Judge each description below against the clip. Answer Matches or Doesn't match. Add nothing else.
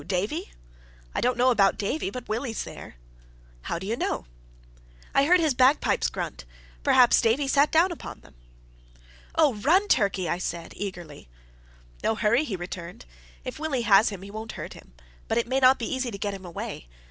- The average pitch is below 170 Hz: Doesn't match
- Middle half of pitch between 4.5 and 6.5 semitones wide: Matches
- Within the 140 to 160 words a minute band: Doesn't match